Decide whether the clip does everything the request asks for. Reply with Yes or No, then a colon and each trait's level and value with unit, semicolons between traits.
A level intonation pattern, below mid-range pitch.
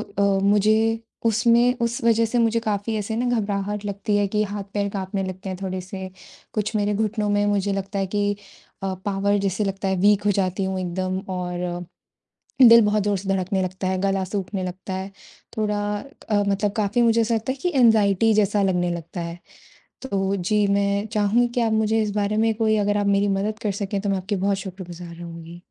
No: narrow, 2.0 semitones; high, 200 Hz